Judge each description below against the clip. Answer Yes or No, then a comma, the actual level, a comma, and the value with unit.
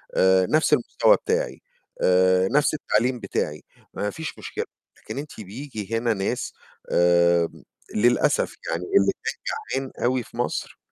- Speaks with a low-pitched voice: Yes, low, 110 Hz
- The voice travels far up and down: Yes, wide, 6.5 semitones